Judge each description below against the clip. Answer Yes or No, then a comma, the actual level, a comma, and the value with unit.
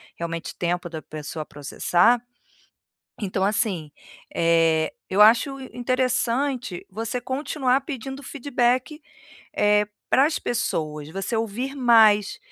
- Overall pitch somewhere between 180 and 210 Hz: No, high, 225 Hz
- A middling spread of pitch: No, wide, 6.7 semitones